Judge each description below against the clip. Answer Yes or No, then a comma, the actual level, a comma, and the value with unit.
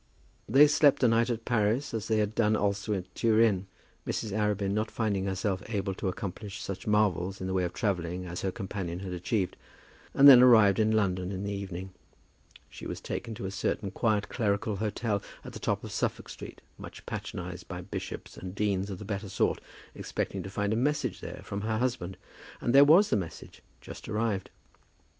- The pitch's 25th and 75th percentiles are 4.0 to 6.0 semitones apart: No, average, 2.7 semitones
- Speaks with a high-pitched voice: No, low, 105 Hz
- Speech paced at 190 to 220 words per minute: Yes, average, 195 wpm